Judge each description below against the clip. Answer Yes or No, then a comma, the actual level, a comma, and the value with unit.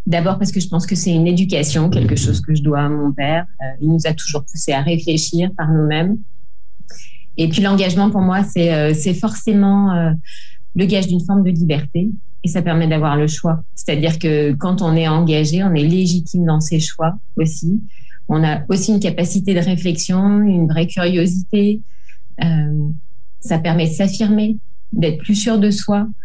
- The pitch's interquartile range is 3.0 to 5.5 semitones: Yes, average, 3.6 semitones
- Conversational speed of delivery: Yes, average, 190 wpm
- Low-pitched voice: No, medium, 170 Hz